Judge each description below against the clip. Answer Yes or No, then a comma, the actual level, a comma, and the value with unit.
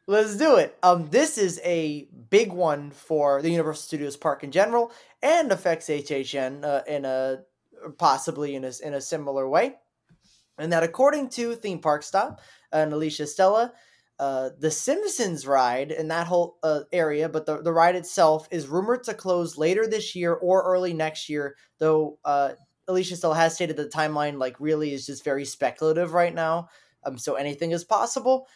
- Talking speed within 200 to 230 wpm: No, average, 180 wpm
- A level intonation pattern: No, average, 3.7 semitones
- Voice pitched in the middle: Yes, medium, 160 Hz